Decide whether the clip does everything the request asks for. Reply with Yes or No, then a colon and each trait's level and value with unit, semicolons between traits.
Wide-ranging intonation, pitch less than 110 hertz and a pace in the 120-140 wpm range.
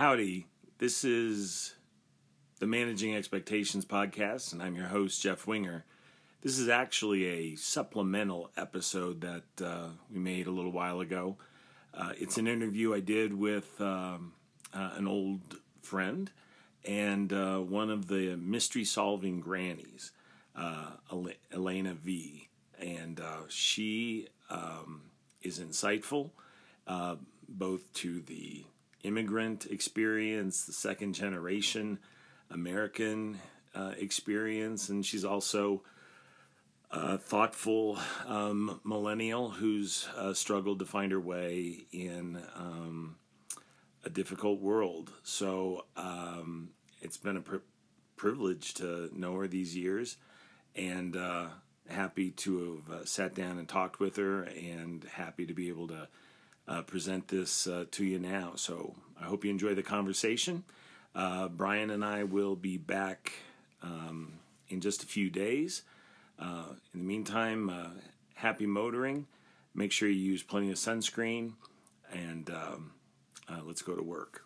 No: average, 2.9 semitones; very low, 95 Hz; slow, 135 wpm